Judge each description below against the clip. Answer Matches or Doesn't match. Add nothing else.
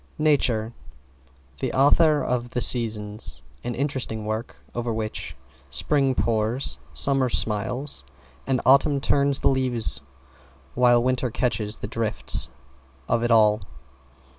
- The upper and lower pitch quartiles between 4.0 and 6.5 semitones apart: Doesn't match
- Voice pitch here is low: Matches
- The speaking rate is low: Matches